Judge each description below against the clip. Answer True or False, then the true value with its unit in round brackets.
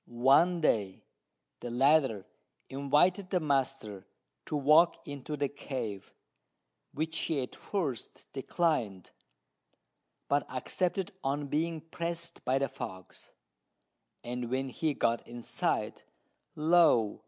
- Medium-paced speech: False (110 wpm)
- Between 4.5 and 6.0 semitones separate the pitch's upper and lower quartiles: True (4.9 semitones)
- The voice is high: False (140 Hz)